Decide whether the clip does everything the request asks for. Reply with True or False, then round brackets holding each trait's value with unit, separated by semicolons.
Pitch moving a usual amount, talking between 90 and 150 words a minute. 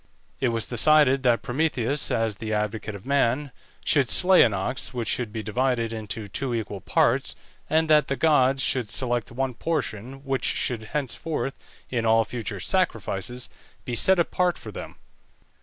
False (3.7 semitones; 160 wpm)